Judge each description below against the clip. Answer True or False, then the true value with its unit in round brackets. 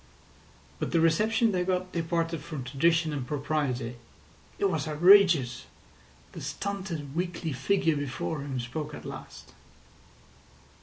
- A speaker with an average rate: False (120 wpm)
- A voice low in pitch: False (160 Hz)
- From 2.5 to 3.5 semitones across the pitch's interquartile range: False (4.1 semitones)